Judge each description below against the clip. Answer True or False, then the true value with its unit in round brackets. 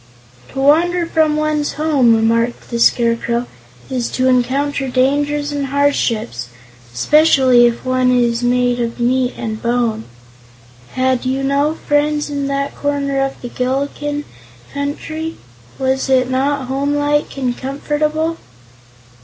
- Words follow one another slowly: True (125 wpm)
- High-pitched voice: True (270 Hz)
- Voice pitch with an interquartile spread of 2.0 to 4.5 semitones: True (2.9 semitones)